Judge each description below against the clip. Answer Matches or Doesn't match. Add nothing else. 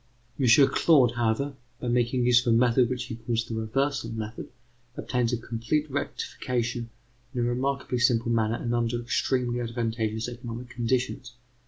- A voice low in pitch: Matches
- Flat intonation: Matches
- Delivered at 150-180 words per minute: Matches